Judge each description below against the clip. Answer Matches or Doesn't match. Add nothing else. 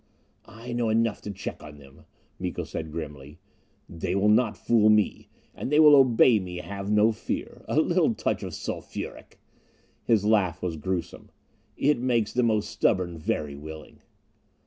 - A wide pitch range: Matches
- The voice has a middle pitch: Doesn't match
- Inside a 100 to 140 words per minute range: Doesn't match